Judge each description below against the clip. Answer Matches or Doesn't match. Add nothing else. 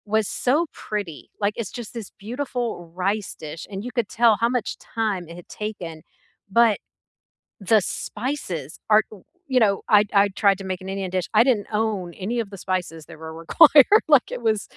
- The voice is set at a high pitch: Matches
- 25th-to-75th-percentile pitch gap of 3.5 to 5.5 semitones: Matches